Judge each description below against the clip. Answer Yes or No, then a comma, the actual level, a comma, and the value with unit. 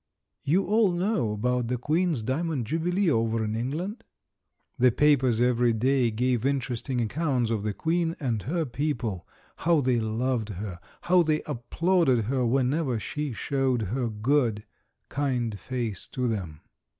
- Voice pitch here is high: No, low, 125 Hz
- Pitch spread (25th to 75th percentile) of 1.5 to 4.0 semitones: No, average, 4.8 semitones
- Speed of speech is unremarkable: Yes, average, 145 wpm